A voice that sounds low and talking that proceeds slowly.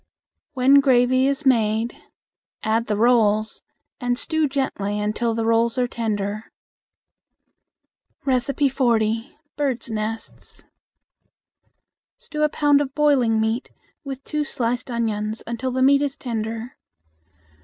No: high, 240 Hz; slow, 110 wpm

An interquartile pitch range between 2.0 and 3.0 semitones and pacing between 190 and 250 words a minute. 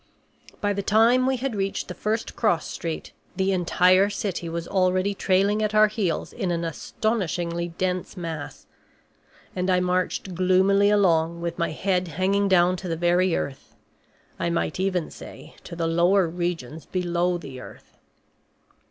No: average, 2.7 semitones; average, 155 wpm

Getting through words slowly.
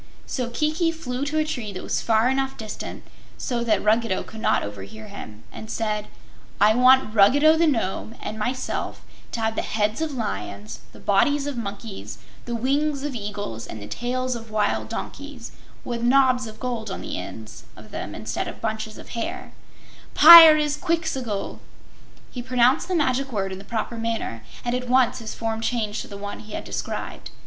No: average, 180 wpm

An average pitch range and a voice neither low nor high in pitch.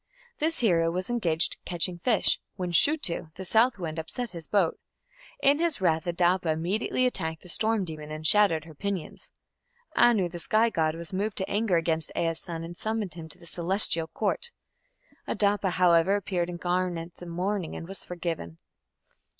Yes: average, 3.7 semitones; medium, 180 Hz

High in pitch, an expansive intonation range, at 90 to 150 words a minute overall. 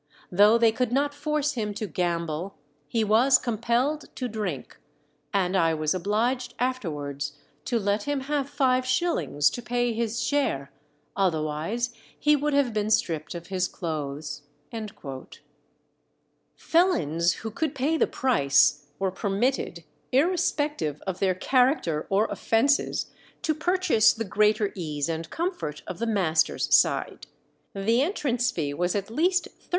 Yes: high, 215 Hz; wide, 7.6 semitones; average, 140 wpm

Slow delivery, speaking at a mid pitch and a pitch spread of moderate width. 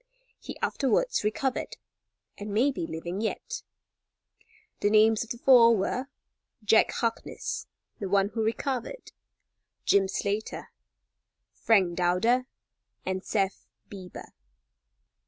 No: slow, 105 wpm; high, 215 Hz; average, 3.5 semitones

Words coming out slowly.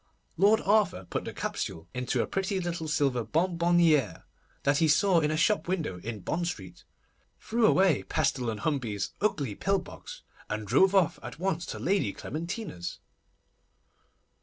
No: average, 155 wpm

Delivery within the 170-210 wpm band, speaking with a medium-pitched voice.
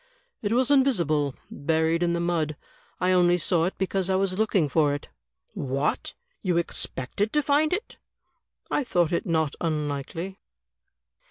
No: average, 150 wpm; medium, 175 Hz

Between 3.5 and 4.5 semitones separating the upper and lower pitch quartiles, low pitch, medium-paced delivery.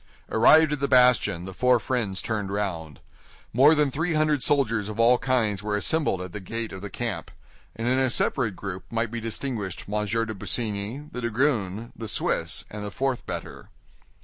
Yes: average, 3.9 semitones; low, 115 Hz; average, 185 wpm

